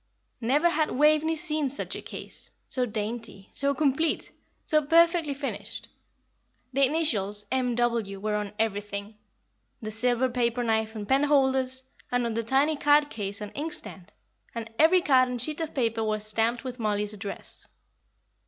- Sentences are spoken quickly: No, average, 155 wpm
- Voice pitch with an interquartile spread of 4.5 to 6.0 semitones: Yes, average, 5.1 semitones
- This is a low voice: No, high, 245 Hz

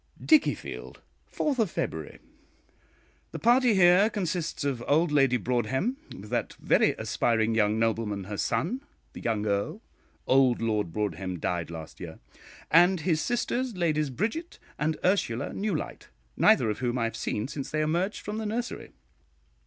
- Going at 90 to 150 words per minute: Yes, average, 145 wpm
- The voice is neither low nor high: Yes, medium, 145 Hz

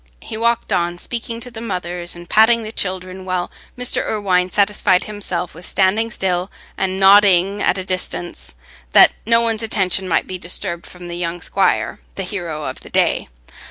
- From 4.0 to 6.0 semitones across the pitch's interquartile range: No, average, 3.0 semitones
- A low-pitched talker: No, medium, 185 Hz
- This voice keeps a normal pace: Yes, average, 175 wpm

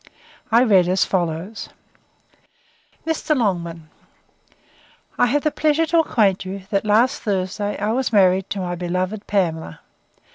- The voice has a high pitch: Yes, high, 200 Hz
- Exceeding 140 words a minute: No, slow, 135 wpm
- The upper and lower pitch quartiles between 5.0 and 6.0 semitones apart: No, average, 4.6 semitones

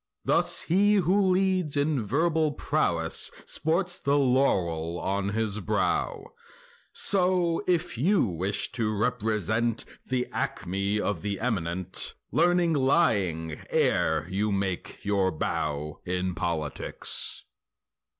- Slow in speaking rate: Yes, slow, 110 wpm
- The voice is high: No, low, 110 Hz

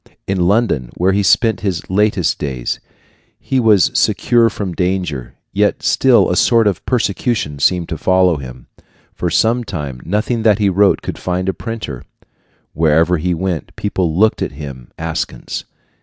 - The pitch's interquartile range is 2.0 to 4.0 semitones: No, average, 4.7 semitones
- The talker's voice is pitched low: Yes, very low, 95 Hz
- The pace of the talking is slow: No, average, 155 wpm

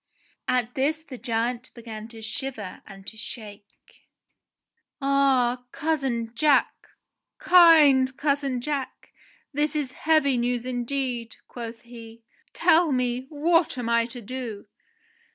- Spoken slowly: Yes, slow, 120 wpm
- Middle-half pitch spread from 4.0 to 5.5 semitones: No, average, 3.2 semitones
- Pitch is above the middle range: Yes, very high, 250 Hz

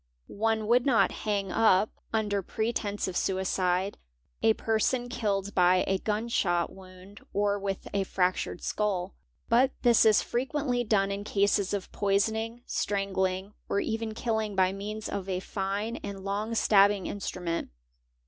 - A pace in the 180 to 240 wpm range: No, average, 140 wpm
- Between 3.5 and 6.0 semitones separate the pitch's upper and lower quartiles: No, narrow, 2.4 semitones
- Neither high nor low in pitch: No, high, 205 Hz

